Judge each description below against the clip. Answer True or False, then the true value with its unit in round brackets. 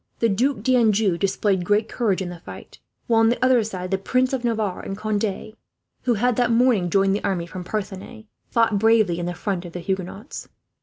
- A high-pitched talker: True (210 Hz)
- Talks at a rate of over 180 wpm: True (205 wpm)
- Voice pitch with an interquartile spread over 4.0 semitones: False (3.4 semitones)